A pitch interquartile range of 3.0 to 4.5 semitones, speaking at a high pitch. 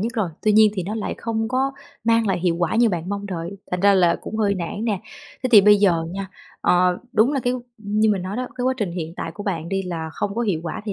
Yes: average, 3.7 semitones; high, 200 Hz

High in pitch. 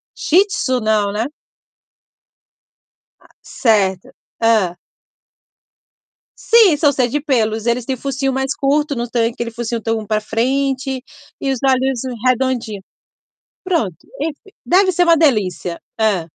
Yes: very high, 250 Hz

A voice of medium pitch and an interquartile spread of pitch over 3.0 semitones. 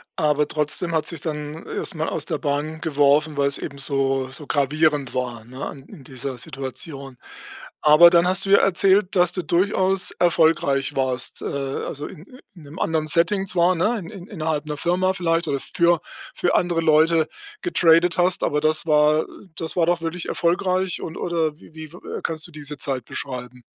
Yes: medium, 155 Hz; average, 3.5 semitones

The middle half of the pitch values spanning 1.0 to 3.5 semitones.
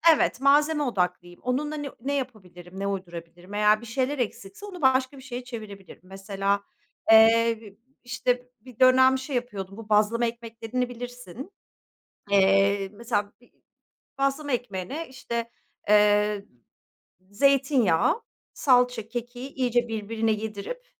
No: average, 4.2 semitones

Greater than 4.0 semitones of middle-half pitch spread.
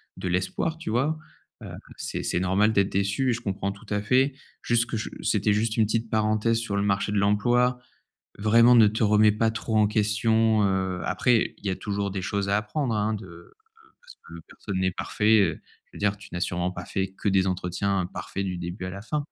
No: narrow, 2.6 semitones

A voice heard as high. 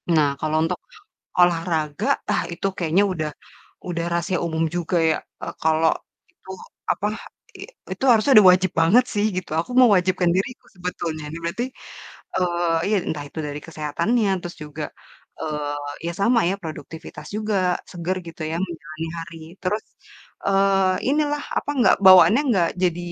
No: medium, 175 Hz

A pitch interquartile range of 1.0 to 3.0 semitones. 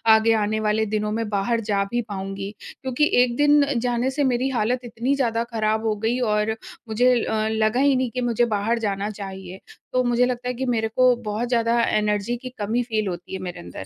Yes: average, 2.7 semitones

